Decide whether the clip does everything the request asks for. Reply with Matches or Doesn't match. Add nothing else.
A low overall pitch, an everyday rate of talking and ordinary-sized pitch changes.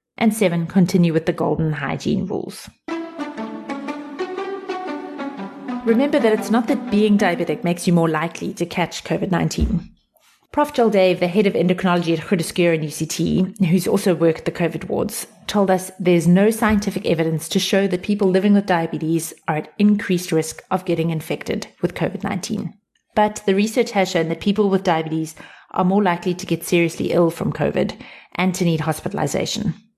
Doesn't match